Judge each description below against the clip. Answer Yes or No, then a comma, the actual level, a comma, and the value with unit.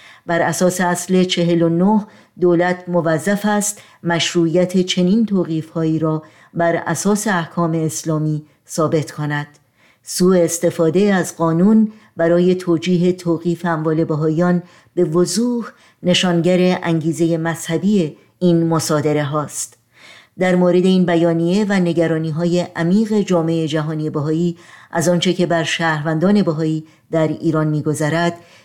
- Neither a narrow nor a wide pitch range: No, narrow, 2.0 semitones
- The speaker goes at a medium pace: Yes, average, 115 wpm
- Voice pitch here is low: No, medium, 170 Hz